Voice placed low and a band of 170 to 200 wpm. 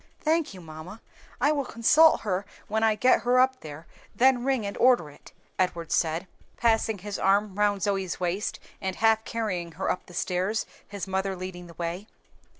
No: high, 200 Hz; average, 180 wpm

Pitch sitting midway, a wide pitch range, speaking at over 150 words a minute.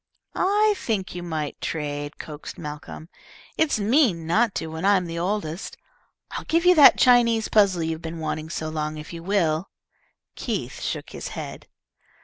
Yes: medium, 170 Hz; wide, 5.8 semitones; average, 160 wpm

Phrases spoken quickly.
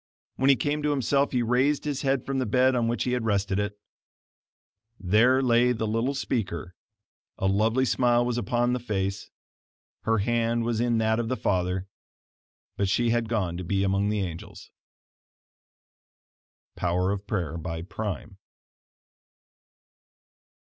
No: average, 150 wpm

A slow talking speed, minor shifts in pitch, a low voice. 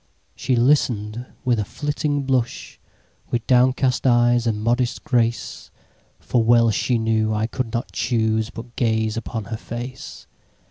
Yes: slow, 125 wpm; narrow, 2.2 semitones; low, 120 Hz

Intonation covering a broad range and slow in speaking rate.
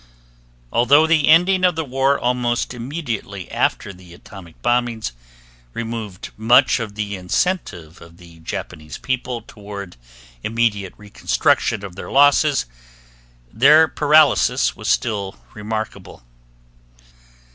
Yes: wide, 5.8 semitones; slow, 110 wpm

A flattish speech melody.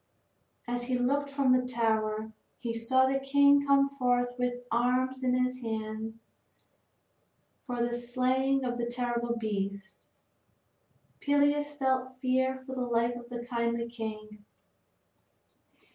Yes: narrow, 1.8 semitones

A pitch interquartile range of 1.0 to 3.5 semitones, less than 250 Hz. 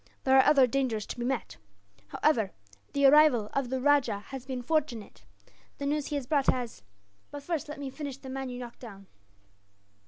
No: average, 2.9 semitones; very high, 265 Hz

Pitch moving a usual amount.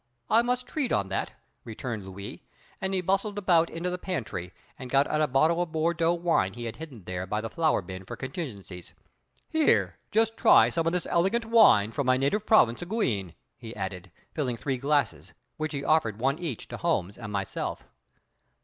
No: wide, 8.5 semitones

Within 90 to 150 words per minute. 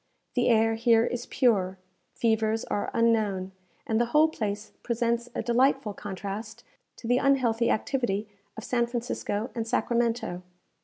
Yes: average, 140 wpm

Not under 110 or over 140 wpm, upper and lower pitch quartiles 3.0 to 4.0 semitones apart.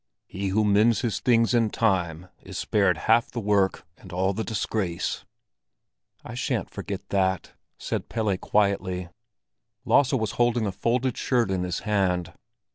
No: average, 150 wpm; average, 3.5 semitones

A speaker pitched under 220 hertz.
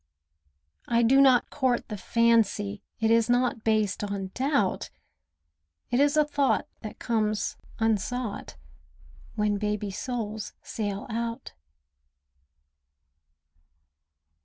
No: high, 225 Hz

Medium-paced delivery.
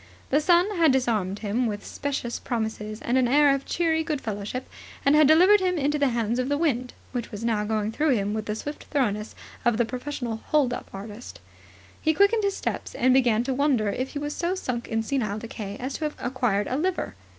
No: fast, 215 wpm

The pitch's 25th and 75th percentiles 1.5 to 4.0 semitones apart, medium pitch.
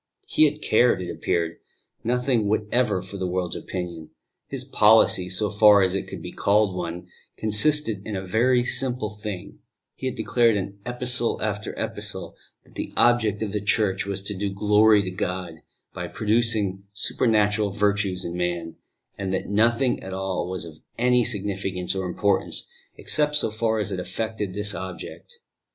No: average, 3.2 semitones; low, 105 Hz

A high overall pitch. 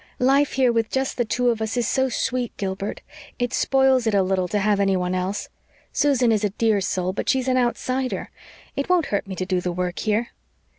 Yes: high, 225 Hz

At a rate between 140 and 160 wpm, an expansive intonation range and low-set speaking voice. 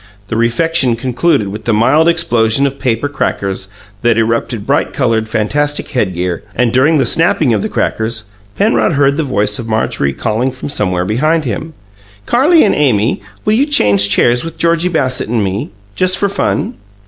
No: average, 170 wpm; wide, 5.9 semitones; low, 120 Hz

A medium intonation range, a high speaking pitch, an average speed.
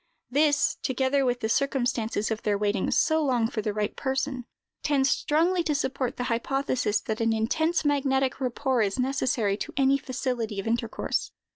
Yes: average, 3.6 semitones; very high, 255 Hz; average, 165 wpm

